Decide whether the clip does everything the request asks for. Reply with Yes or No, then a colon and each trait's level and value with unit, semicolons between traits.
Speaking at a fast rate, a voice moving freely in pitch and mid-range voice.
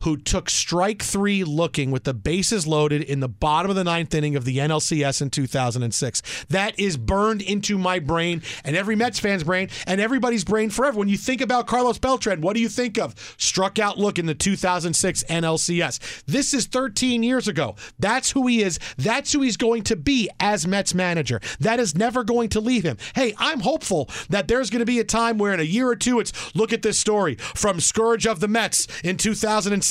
No: fast, 215 wpm; wide, 6.0 semitones; high, 200 Hz